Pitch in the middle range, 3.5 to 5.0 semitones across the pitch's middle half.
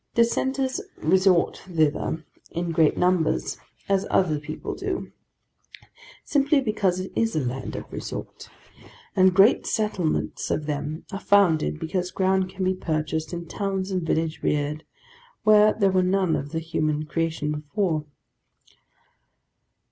Yes: medium, 180 Hz; average, 3.9 semitones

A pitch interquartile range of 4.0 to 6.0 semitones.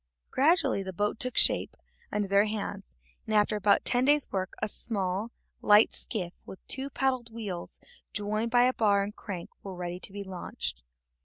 No: average, 3.3 semitones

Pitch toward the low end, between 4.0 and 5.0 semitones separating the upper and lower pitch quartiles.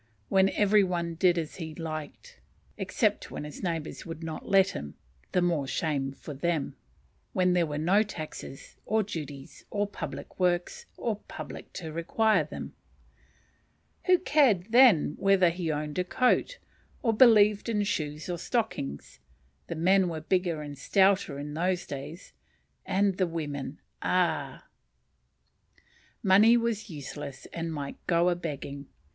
No: medium, 175 Hz; average, 4.5 semitones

